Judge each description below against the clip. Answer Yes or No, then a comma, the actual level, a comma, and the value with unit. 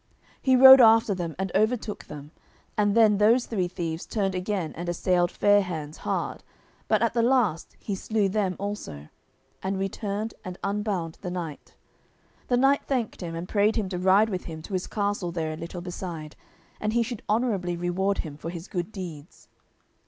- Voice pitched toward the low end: No, high, 195 Hz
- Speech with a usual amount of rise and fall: Yes, average, 3.7 semitones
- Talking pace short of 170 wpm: No, average, 180 wpm